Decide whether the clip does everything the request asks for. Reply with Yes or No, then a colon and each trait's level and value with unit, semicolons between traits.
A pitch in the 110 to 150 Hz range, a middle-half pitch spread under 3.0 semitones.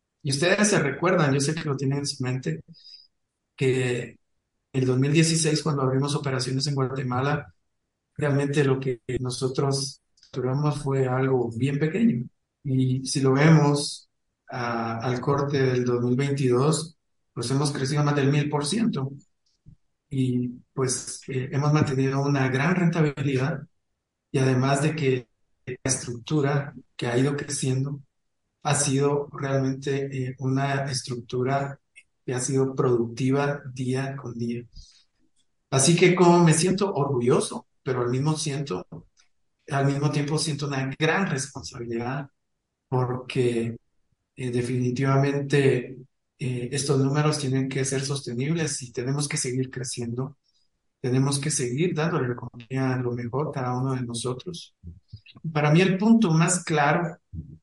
Yes: low, 135 Hz; narrow, 2.5 semitones